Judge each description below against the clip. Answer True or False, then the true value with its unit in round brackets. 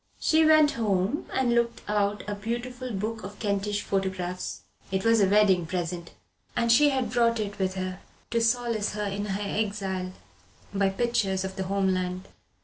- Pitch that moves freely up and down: False (3.4 semitones)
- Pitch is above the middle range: True (205 Hz)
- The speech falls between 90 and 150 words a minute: False (170 wpm)